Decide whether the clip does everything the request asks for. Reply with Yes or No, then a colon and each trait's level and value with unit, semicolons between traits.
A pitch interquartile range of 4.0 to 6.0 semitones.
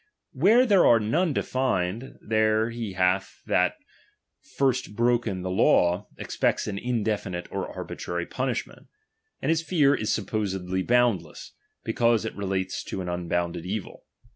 Yes: average, 4.7 semitones